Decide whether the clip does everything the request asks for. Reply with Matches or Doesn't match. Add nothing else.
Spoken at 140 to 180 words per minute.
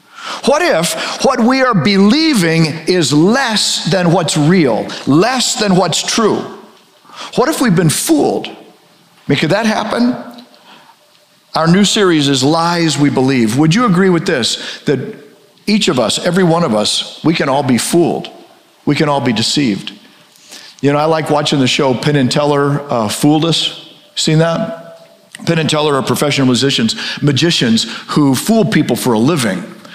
Matches